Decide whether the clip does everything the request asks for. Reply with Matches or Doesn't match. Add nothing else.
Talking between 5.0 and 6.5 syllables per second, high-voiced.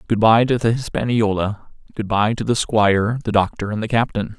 Doesn't match